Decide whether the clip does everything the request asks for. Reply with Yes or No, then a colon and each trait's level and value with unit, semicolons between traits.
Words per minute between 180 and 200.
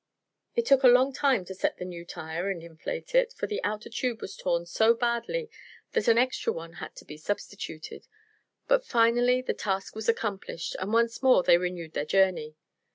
Yes: average, 195 wpm